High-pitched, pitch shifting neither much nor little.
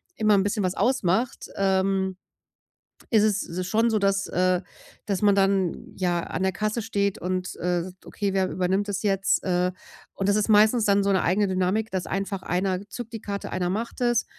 No: high, 195 Hz; narrow, 2.1 semitones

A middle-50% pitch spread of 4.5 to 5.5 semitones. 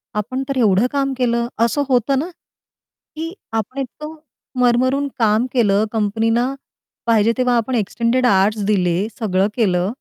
No: average, 3.5 semitones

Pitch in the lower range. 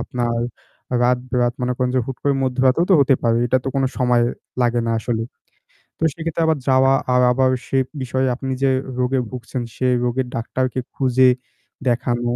Yes: low, 130 Hz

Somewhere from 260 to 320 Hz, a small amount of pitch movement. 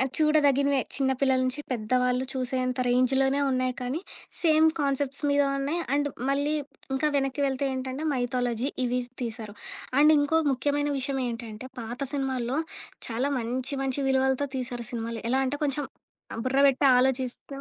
Yes: very high, 265 Hz; narrow, 2.1 semitones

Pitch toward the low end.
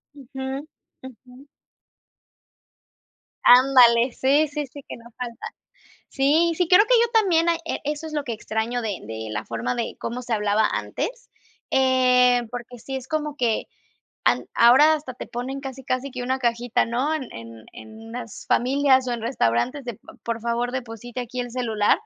No: very high, 250 Hz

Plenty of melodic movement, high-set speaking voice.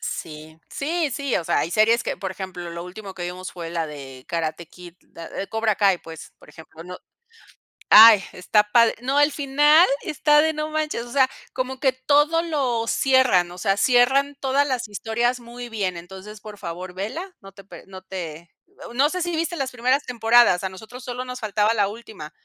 Yes: wide, 6.5 semitones; high, 220 Hz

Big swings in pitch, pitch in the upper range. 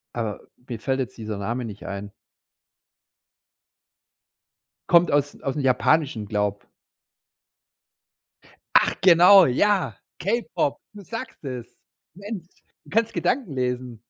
No: wide, 7.8 semitones; low, 135 Hz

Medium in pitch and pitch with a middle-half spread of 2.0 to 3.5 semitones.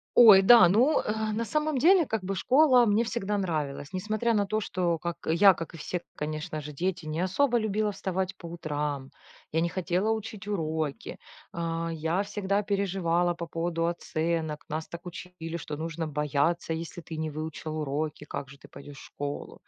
No: medium, 170 Hz; average, 4.5 semitones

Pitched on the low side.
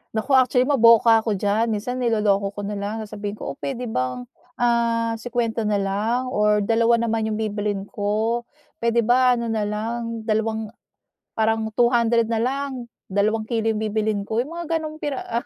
No: high, 225 Hz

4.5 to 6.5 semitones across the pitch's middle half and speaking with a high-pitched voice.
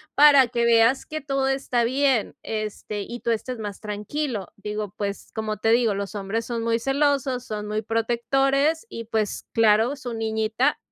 No: average, 3.9 semitones; high, 230 Hz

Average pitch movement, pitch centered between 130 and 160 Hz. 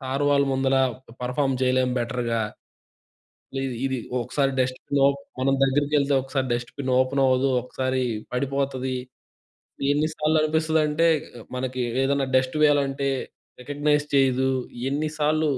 No: narrow, 2.0 semitones; low, 135 Hz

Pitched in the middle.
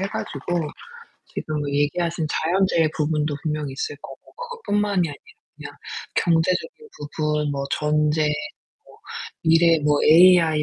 Yes: medium, 160 Hz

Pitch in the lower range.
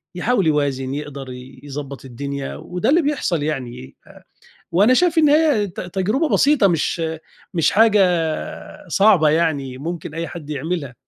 No: medium, 165 Hz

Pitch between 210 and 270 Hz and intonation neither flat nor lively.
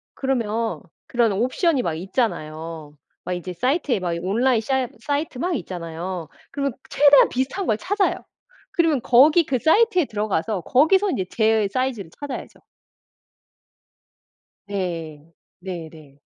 No: high, 230 Hz; wide, 7.7 semitones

